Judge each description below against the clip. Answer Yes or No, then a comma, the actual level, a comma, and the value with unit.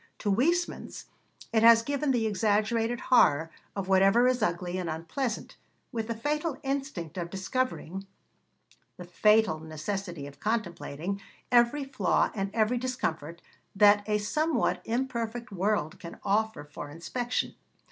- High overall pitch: Yes, high, 215 Hz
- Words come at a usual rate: No, slow, 130 wpm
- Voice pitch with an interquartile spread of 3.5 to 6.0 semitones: Yes, wide, 5.4 semitones